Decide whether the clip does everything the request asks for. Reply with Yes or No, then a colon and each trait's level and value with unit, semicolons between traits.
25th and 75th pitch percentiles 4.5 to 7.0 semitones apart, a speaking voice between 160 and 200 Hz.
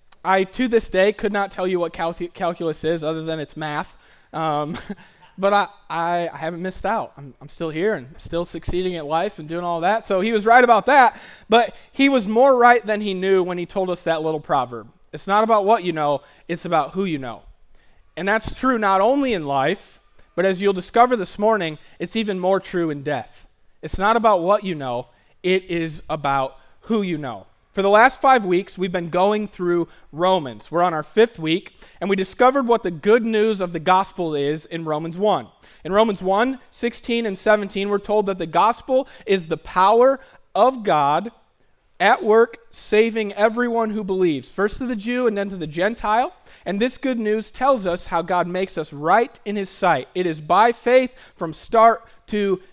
Yes: average, 4.8 semitones; high, 190 Hz